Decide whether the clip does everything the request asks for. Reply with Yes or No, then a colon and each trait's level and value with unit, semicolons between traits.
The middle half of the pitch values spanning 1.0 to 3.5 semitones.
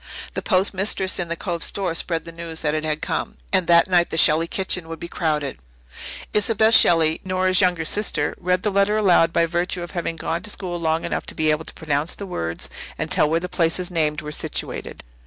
Yes: narrow, 2.4 semitones